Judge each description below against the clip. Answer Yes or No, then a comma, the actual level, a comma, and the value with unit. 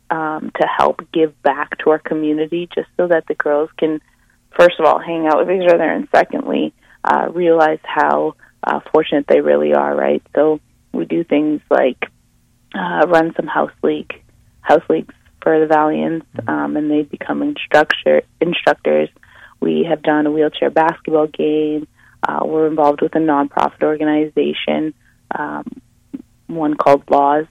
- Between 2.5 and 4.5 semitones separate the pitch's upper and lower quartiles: No, average, 5.0 semitones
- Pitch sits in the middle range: Yes, medium, 150 Hz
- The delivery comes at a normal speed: Yes, average, 155 wpm